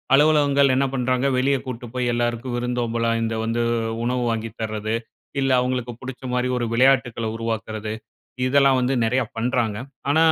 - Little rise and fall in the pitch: Yes, narrow, 2.2 semitones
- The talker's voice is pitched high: No, low, 125 Hz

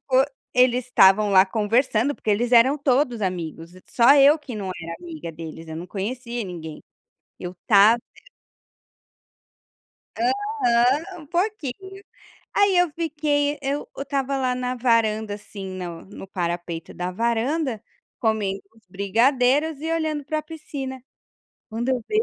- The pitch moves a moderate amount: No, wide, 6.4 semitones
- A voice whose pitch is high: Yes, high, 245 Hz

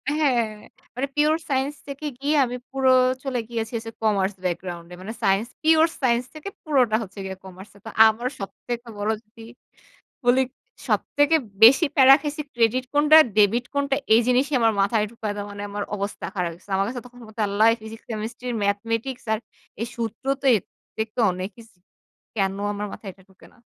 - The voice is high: Yes, high, 230 Hz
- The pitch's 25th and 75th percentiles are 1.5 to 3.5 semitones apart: No, average, 4.6 semitones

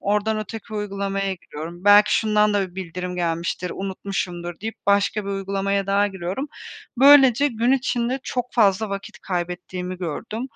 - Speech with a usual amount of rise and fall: Yes, average, 3.1 semitones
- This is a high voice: Yes, high, 200 Hz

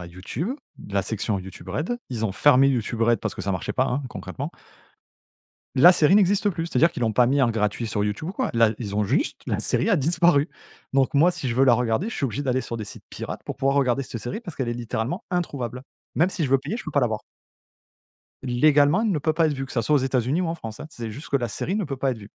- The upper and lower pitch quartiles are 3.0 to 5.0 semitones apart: No, wide, 5.5 semitones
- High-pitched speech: No, low, 130 Hz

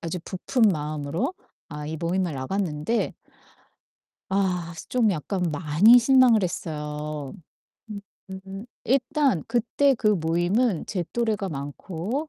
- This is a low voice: No, high, 190 Hz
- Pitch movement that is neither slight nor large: No, wide, 6.4 semitones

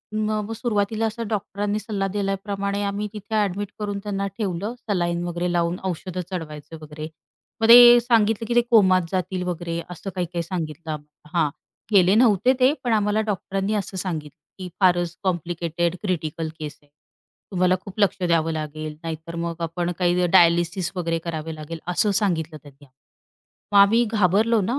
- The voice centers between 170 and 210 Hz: Yes, medium, 185 Hz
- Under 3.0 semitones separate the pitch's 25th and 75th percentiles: No, average, 3.6 semitones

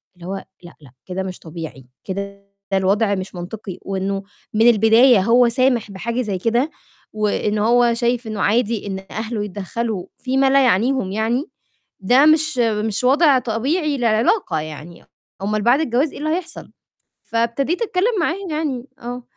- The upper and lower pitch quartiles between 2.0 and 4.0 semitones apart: No, average, 4.6 semitones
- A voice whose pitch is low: No, high, 230 Hz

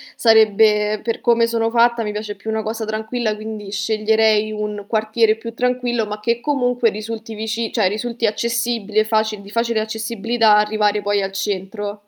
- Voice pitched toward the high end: Yes, high, 220 Hz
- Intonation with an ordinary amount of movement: No, narrow, 1.6 semitones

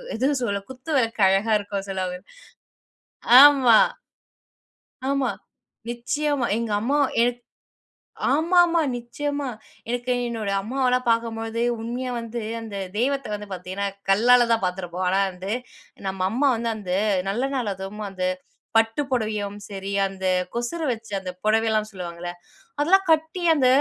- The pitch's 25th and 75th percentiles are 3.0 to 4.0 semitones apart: No, average, 4.5 semitones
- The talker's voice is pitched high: Yes, high, 225 Hz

